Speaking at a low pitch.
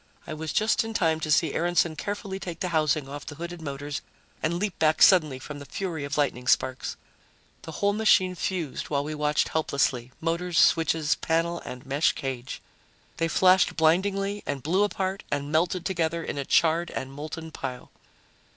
No: medium, 160 Hz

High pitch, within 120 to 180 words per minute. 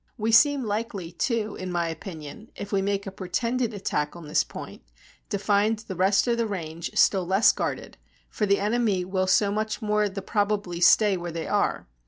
No: high, 200 Hz; average, 195 wpm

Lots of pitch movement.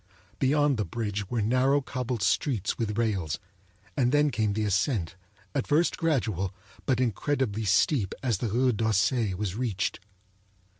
No: average, 4.5 semitones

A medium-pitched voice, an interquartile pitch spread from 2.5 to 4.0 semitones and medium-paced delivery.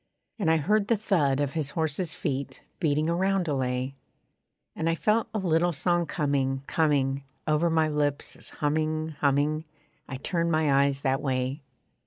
Yes: medium, 155 Hz; average, 3.2 semitones; average, 160 wpm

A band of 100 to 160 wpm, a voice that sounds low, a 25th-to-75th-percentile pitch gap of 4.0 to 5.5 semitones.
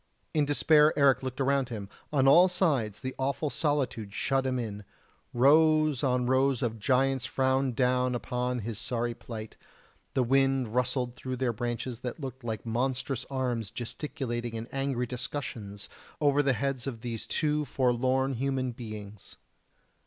No: average, 150 wpm; low, 130 Hz; narrow, 2.5 semitones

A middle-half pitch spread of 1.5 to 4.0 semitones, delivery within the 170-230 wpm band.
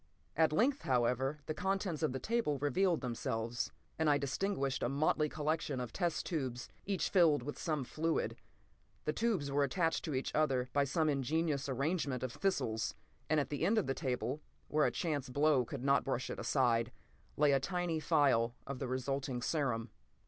Yes: average, 3.6 semitones; average, 180 wpm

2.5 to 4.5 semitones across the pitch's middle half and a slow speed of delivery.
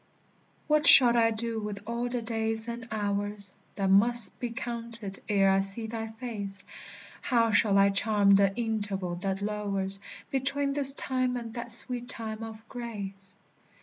No: average, 3.0 semitones; average, 155 wpm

